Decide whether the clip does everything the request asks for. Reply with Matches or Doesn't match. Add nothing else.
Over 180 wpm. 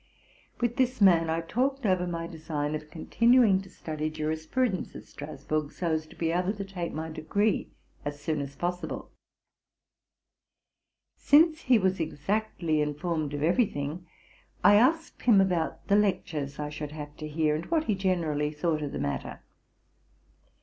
Doesn't match